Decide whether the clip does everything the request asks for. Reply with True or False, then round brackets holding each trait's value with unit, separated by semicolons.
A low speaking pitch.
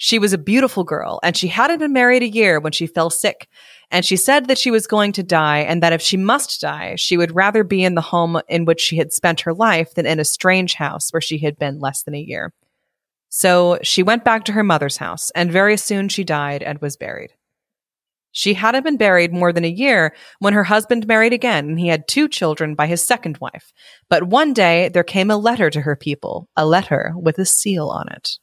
False (180 Hz)